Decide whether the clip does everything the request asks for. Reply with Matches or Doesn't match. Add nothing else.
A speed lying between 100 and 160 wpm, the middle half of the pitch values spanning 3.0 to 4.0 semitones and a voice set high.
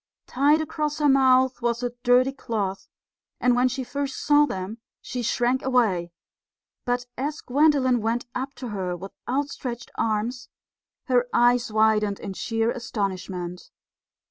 Matches